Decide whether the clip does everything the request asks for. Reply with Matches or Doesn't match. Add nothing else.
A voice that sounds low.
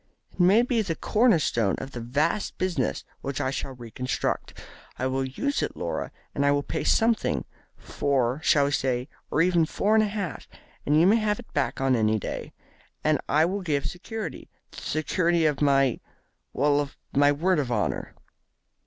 Doesn't match